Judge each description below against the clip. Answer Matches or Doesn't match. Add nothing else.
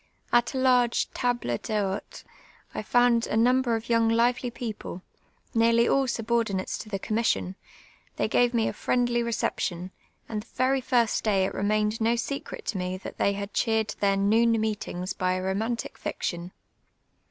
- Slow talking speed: Doesn't match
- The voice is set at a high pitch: Matches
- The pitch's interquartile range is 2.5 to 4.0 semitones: Matches